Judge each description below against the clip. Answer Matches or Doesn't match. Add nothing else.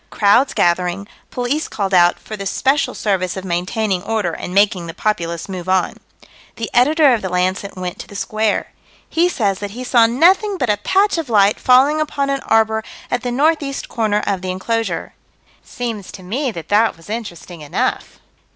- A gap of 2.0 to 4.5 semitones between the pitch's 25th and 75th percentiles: Doesn't match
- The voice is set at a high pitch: Matches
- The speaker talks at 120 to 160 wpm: Doesn't match